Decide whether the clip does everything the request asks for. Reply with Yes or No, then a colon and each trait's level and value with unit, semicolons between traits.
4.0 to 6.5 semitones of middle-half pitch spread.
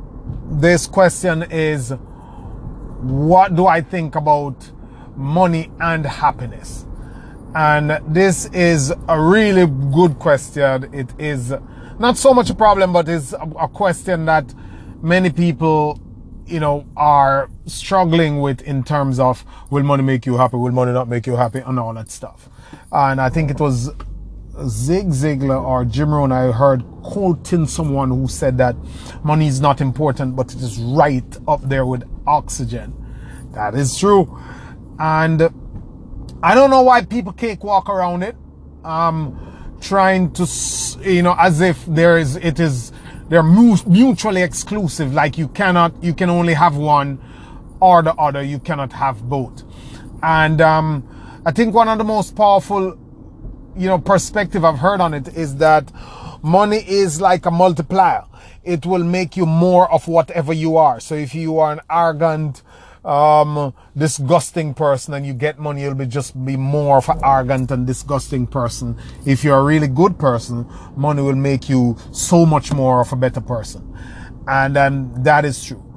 Yes: average, 4.7 semitones